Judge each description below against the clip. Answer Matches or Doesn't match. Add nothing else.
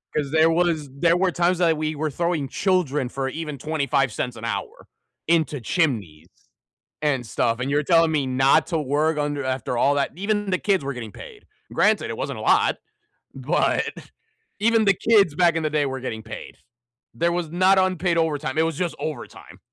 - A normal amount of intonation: Matches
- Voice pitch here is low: Doesn't match